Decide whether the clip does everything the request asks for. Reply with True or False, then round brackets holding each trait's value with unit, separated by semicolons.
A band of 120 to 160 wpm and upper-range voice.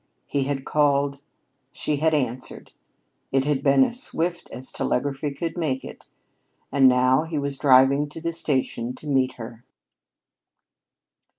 False (140 wpm; 140 Hz)